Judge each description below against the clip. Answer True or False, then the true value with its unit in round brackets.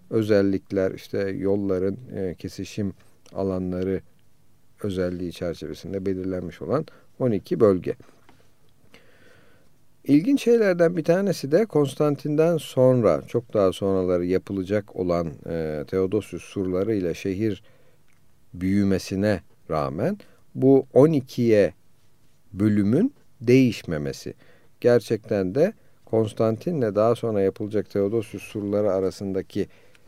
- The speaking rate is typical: False (90 wpm)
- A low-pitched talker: True (100 Hz)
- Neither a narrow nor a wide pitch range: True (4.1 semitones)